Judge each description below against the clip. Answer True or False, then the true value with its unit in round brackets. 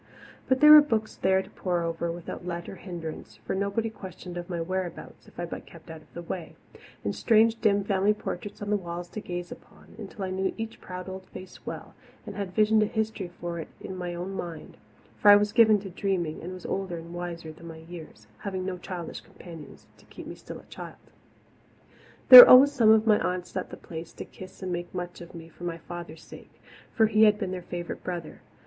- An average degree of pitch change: True (3.2 semitones)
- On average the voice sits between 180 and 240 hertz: True (185 Hz)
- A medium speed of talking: False (225 wpm)